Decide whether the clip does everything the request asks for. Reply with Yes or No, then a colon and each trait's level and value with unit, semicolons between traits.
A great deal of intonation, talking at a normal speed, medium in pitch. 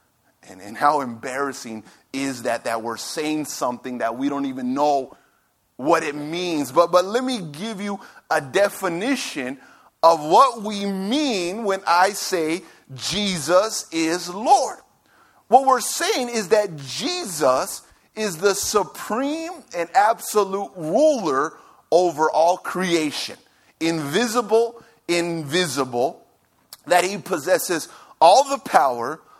No: wide, 6.4 semitones; slow, 120 wpm; medium, 180 Hz